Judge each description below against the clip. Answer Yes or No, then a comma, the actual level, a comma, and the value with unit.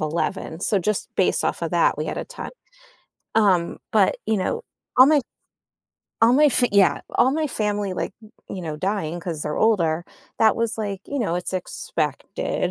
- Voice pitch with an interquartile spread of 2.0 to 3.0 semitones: No, average, 4.7 semitones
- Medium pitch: No, high, 200 Hz